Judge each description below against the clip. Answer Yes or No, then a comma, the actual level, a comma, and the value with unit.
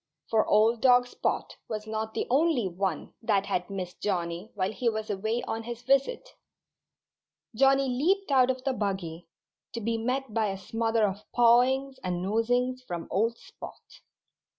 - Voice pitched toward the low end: No, high, 225 Hz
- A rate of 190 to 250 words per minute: No, average, 160 wpm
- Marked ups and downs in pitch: No, average, 4.2 semitones